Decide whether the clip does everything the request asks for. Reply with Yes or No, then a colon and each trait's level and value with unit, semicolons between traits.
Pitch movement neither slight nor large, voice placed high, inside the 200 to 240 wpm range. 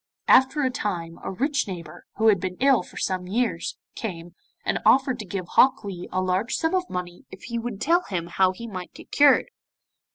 No: wide, 6.1 semitones; high, 200 Hz; fast, 205 wpm